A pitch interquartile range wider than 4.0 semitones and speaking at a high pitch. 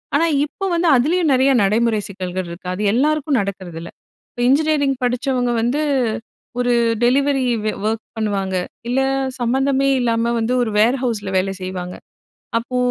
Yes: average, 5.2 semitones; high, 240 Hz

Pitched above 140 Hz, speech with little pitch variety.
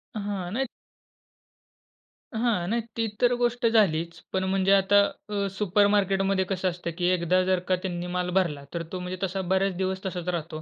Yes: high, 190 Hz; narrow, 2.2 semitones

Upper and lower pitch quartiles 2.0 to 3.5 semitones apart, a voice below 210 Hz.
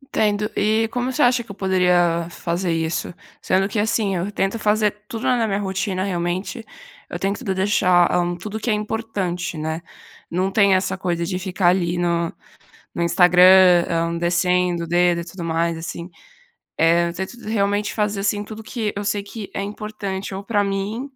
Yes: average, 3.2 semitones; high, 190 Hz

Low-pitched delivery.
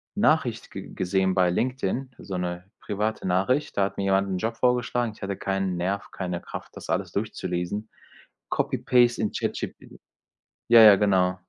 Yes: low, 100 Hz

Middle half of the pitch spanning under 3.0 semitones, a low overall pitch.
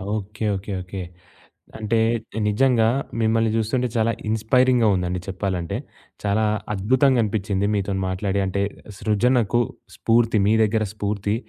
Yes: narrow, 2.5 semitones; low, 105 Hz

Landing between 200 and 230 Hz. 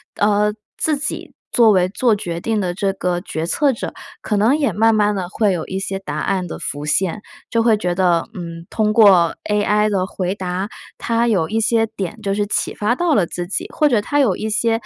Yes: high, 205 Hz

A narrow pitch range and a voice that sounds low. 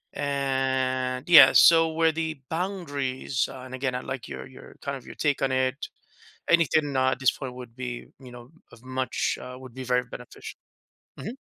Yes: narrow, 2.0 semitones; low, 130 Hz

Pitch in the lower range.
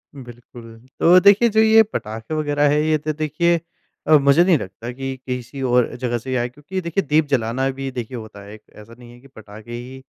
Yes: low, 130 Hz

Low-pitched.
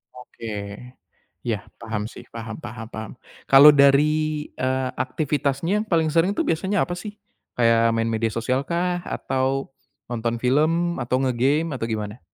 Yes: low, 130 Hz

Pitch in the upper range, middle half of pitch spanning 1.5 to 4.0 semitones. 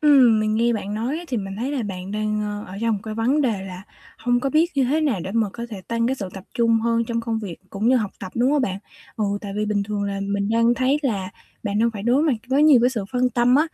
Yes: high, 230 Hz; average, 3.5 semitones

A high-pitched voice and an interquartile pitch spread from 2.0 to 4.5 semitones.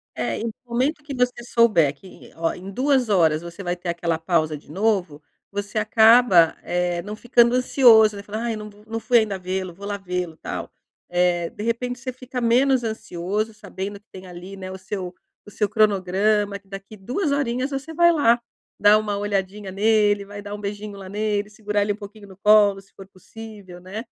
Yes: high, 205 Hz; average, 3.3 semitones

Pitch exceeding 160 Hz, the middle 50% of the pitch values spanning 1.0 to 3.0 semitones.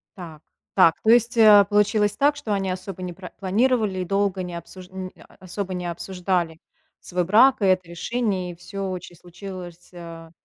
Yes: medium, 185 Hz; average, 2.7 semitones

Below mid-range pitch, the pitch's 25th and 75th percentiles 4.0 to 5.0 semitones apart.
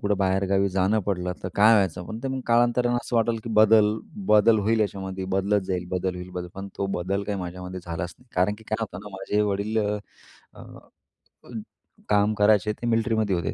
No: low, 100 Hz; average, 2.8 semitones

